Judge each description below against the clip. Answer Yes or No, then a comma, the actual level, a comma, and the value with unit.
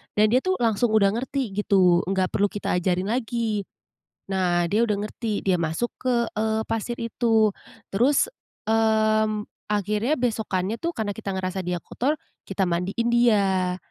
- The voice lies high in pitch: Yes, high, 215 Hz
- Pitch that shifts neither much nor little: Yes, average, 3.5 semitones